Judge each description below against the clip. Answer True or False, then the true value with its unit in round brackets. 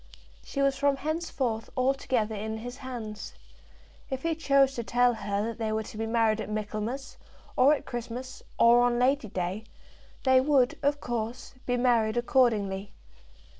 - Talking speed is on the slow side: False (160 wpm)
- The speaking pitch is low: False (245 Hz)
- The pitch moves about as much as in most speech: True (3.4 semitones)